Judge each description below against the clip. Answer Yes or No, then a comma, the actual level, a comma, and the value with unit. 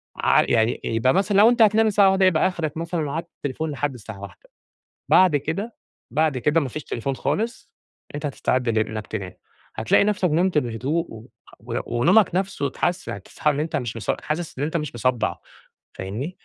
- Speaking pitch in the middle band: Yes, medium, 150 Hz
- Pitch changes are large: Yes, wide, 6.9 semitones